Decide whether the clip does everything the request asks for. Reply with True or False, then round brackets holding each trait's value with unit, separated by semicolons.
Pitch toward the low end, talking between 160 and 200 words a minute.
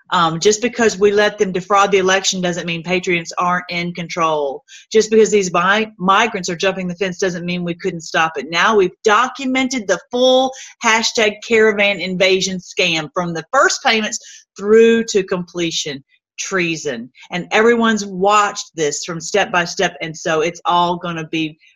False (190 Hz; 170 wpm)